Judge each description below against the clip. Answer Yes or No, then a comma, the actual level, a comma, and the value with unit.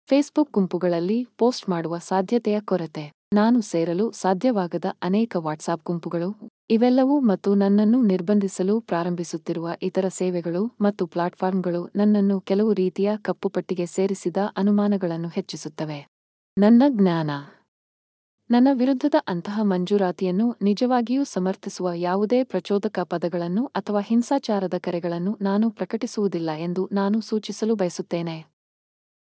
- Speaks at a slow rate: No, average, 100 wpm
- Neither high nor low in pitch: No, high, 195 Hz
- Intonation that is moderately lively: Yes, average, 3.5 semitones